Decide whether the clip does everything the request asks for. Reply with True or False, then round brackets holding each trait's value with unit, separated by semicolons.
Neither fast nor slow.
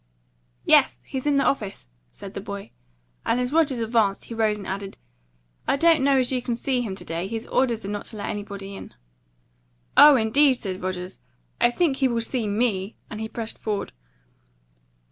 True (190 wpm)